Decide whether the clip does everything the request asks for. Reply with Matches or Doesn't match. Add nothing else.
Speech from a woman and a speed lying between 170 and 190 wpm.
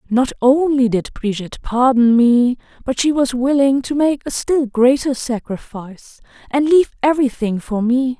Doesn't match